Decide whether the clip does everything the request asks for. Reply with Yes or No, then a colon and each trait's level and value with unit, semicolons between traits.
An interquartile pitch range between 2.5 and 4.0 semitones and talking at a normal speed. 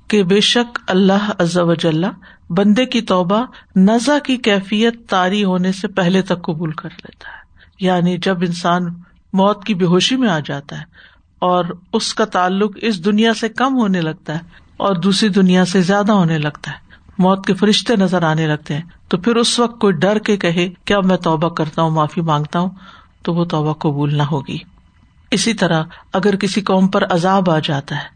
No: average, 3.4 semitones; fast, 195 wpm